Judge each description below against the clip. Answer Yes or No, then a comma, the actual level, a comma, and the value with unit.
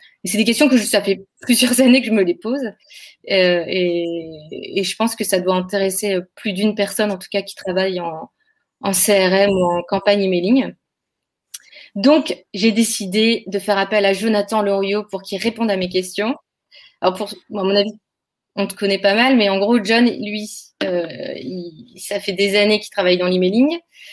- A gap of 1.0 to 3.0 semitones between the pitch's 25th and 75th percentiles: Yes, average, 2.7 semitones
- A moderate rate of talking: Yes, average, 195 wpm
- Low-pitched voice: No, high, 200 Hz